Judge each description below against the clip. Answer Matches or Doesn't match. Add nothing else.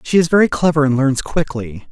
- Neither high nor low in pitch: Matches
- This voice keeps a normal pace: Doesn't match